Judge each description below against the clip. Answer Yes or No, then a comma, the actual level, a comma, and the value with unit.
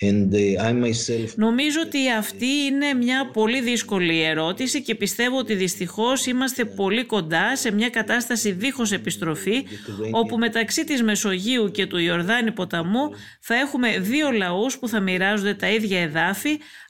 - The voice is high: Yes, high, 220 Hz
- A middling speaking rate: Yes, average, 135 wpm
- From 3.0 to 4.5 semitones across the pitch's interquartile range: No, average, 5.2 semitones